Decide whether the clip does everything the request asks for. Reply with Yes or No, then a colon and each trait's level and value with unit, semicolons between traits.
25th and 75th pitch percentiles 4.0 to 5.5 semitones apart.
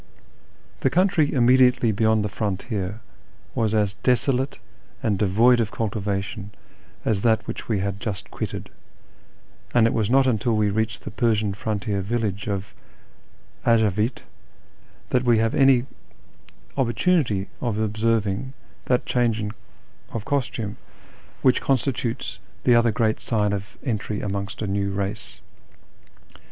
No: average, 3.0 semitones